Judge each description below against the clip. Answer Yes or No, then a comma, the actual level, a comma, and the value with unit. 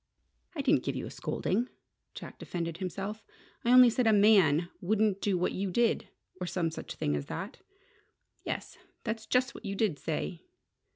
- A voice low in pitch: No, high, 200 Hz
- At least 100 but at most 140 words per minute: No, average, 175 wpm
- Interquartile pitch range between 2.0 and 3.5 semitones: No, average, 4.2 semitones